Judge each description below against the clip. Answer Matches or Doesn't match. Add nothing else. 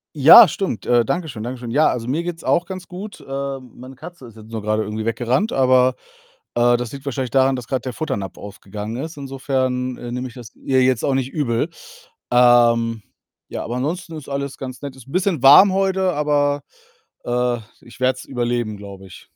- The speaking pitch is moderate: Doesn't match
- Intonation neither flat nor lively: Matches